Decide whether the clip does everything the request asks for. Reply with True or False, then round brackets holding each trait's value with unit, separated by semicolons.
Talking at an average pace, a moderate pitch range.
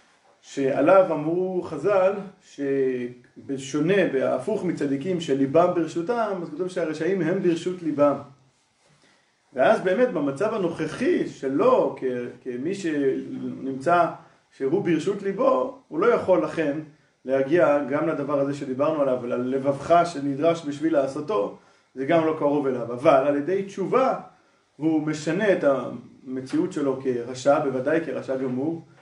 True (120 wpm; 4.6 semitones)